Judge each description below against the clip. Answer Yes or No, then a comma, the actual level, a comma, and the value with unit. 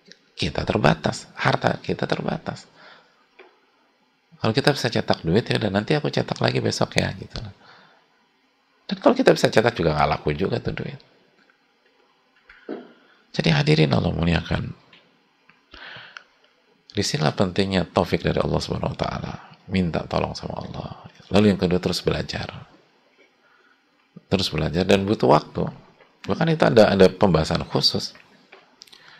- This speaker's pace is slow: Yes, slow, 125 wpm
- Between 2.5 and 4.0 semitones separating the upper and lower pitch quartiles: No, average, 4.8 semitones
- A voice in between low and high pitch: No, low, 100 Hz